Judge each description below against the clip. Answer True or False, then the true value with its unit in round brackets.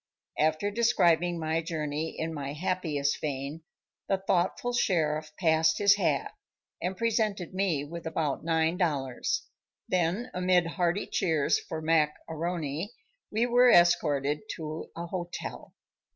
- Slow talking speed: True (125 wpm)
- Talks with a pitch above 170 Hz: False (165 Hz)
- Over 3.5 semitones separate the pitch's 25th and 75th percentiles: False (3.1 semitones)